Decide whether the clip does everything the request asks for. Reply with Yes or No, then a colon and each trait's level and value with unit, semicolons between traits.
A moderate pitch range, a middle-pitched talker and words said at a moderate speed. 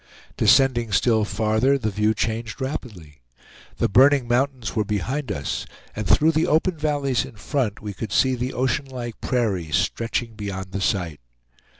No: average, 4.2 semitones; low, 115 Hz; average, 160 wpm